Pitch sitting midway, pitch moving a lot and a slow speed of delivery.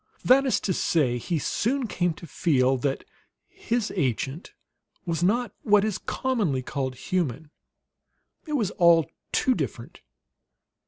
Yes: medium, 175 Hz; wide, 7.8 semitones; slow, 130 wpm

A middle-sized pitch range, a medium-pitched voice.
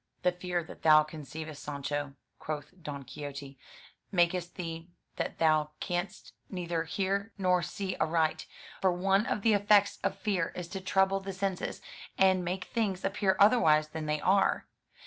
Yes: average, 3.8 semitones; medium, 175 Hz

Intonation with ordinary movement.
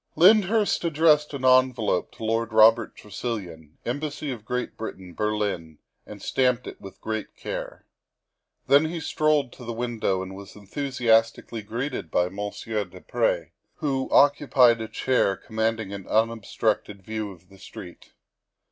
Yes: average, 4.5 semitones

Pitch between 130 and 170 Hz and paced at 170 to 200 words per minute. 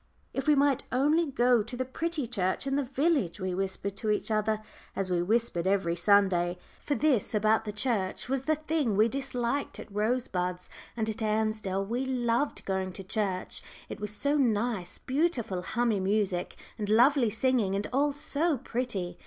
No: high, 220 Hz; average, 175 wpm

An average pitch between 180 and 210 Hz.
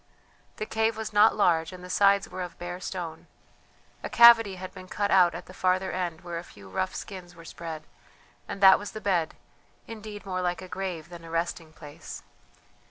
Yes: medium, 185 Hz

